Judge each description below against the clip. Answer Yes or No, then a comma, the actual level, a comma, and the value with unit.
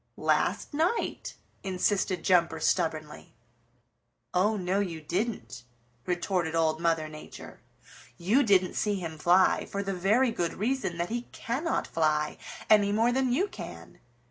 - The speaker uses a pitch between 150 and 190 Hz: Yes, medium, 185 Hz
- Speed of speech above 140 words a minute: No, slow, 135 wpm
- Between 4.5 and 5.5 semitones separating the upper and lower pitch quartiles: Yes, average, 5.0 semitones